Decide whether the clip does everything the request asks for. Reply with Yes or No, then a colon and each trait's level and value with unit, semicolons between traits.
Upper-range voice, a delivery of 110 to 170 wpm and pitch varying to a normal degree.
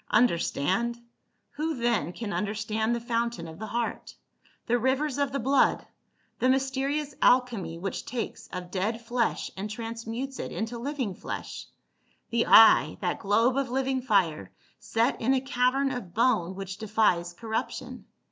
Yes: high, 230 Hz; average, 150 wpm; average, 4.1 semitones